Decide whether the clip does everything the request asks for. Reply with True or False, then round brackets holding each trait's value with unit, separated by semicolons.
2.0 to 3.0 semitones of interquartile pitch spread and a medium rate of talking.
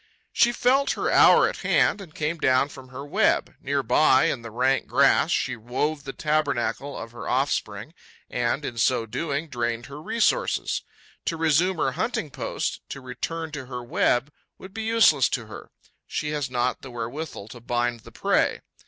False (4.3 semitones; 180 wpm)